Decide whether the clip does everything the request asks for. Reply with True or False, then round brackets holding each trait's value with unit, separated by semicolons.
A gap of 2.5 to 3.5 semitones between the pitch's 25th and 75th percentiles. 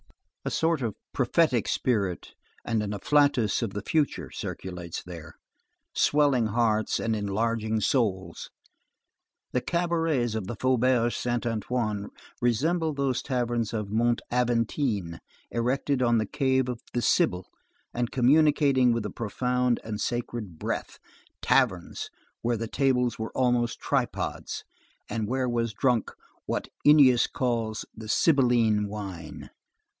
True (3.1 semitones)